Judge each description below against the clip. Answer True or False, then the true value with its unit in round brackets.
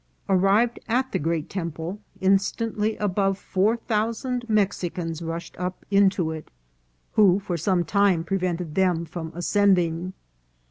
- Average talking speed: False (125 wpm)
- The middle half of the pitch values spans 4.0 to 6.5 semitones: False (3.4 semitones)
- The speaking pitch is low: False (190 Hz)